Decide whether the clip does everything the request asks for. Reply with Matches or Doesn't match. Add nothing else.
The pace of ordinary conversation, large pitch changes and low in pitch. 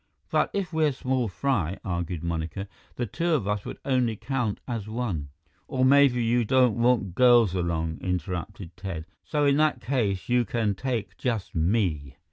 Matches